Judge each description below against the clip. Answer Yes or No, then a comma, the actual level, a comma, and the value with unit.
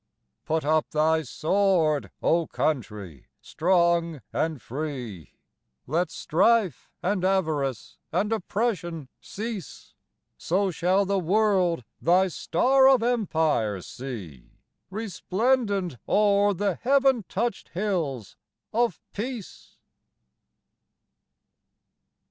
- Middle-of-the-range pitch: Yes, medium, 180 Hz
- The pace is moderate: No, slow, 90 wpm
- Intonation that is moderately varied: Yes, average, 4.9 semitones